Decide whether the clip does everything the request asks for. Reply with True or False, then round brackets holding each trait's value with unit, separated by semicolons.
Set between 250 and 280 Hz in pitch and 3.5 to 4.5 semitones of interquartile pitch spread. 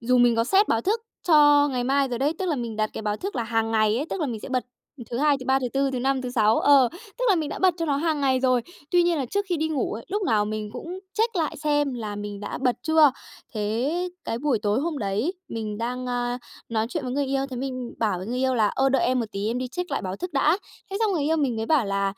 False (255 Hz; 4.9 semitones)